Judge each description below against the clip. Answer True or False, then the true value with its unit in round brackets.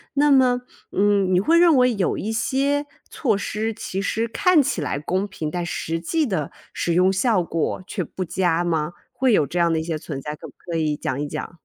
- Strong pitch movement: True (6.9 semitones)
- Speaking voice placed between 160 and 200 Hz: True (190 Hz)